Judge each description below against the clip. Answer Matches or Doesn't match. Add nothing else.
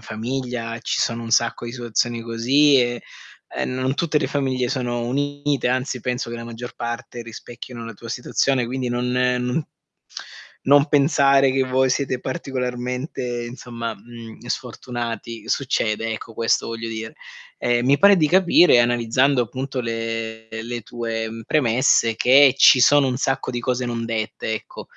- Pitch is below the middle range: Matches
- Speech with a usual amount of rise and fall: Doesn't match